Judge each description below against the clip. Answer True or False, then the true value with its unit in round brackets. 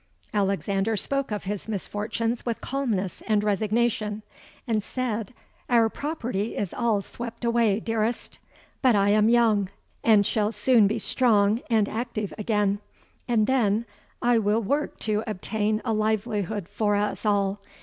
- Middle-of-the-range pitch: False (215 Hz)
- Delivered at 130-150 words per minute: True (140 wpm)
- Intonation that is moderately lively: False (2.2 semitones)